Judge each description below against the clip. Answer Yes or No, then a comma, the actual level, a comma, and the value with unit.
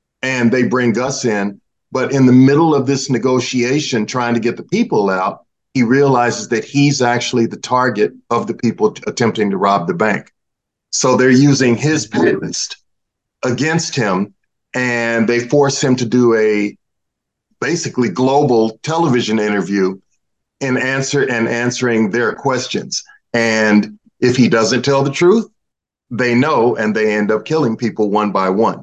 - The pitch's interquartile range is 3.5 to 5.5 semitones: No, average, 3.1 semitones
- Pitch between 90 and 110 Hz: No, low, 125 Hz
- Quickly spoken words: No, average, 155 wpm